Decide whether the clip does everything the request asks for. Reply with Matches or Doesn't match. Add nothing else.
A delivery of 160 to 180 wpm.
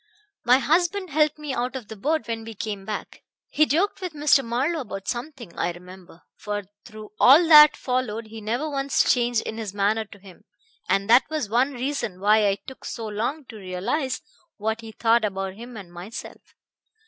Doesn't match